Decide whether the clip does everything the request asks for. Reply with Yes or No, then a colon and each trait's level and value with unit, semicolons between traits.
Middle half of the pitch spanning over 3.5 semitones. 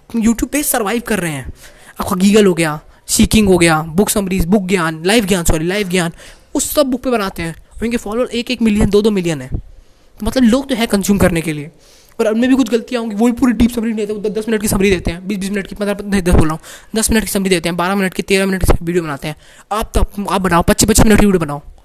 Yes: average, 4.3 semitones